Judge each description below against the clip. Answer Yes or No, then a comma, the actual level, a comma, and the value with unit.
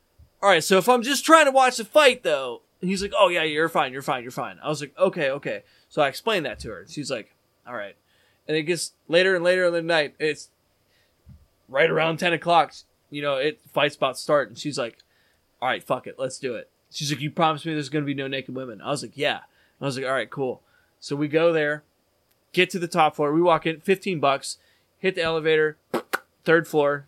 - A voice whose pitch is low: No, medium, 155 Hz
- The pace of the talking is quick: Yes, fast, 235 wpm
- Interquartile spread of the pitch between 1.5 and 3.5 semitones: No, average, 4.6 semitones